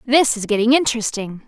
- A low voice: No, high, 230 Hz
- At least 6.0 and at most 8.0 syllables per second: Yes, 6.1 syllables/s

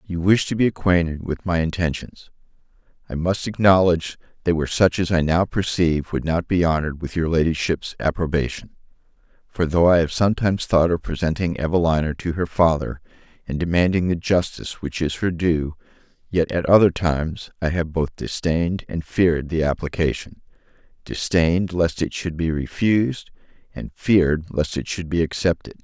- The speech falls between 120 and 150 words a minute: No, average, 165 wpm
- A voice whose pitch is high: No, very low, 85 Hz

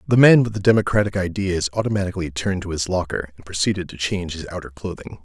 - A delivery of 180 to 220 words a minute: Yes, fast, 205 wpm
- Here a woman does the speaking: No, male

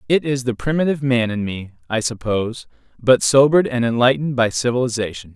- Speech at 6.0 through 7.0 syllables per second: Yes, 6.2 syllables/s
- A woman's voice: No, male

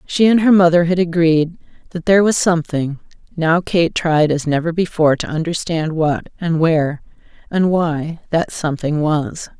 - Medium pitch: Yes, medium, 165 Hz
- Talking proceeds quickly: No, average, 165 wpm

